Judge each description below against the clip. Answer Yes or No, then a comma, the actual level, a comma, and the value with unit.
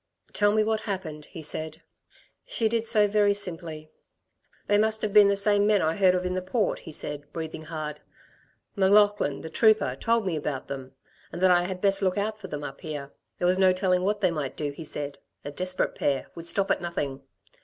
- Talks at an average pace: No, fast, 215 wpm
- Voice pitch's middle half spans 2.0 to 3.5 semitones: No, average, 4.9 semitones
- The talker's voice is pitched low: No, medium, 185 Hz